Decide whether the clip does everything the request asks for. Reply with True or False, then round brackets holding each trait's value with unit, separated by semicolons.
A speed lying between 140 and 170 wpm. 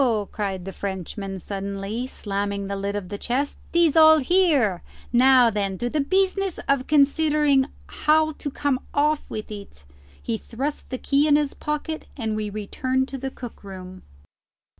True (160 wpm)